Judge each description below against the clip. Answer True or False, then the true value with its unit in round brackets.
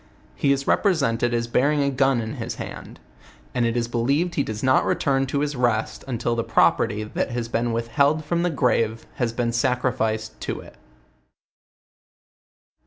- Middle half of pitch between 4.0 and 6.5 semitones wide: False (3.2 semitones)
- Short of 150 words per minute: False (170 wpm)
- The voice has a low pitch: True (125 Hz)